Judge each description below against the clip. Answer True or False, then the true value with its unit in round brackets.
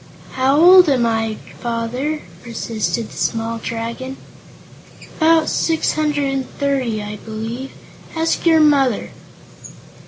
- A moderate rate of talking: False (115 wpm)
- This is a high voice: True (260 Hz)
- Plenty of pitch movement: False (4.8 semitones)